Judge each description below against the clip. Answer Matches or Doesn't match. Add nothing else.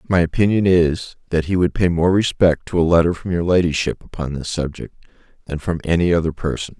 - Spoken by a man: Matches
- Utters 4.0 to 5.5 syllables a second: Doesn't match